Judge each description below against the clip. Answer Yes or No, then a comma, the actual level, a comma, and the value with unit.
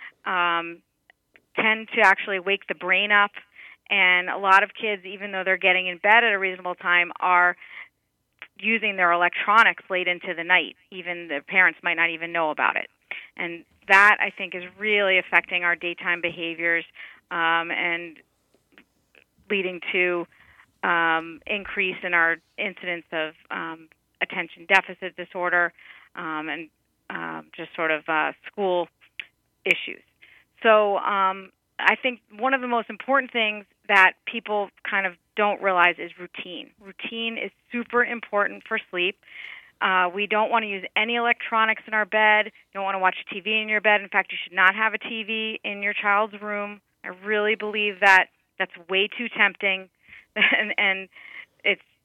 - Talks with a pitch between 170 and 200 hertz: Yes, high, 190 Hz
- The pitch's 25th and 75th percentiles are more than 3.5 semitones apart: No, average, 3.2 semitones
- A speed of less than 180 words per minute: Yes, average, 160 wpm